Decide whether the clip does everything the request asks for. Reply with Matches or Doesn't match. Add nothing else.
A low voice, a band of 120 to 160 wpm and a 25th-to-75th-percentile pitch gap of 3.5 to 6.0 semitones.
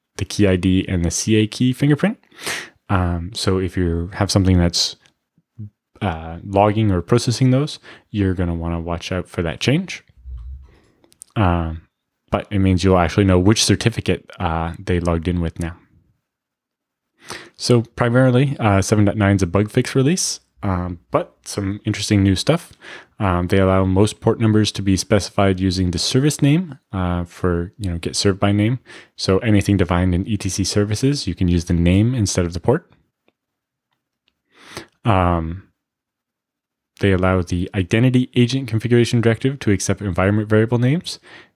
Matches